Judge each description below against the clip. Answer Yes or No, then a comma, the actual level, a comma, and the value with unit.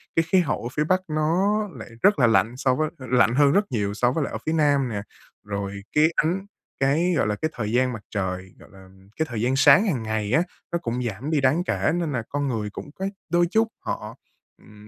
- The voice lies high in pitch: No, low, 130 Hz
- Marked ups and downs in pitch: Yes, wide, 6.5 semitones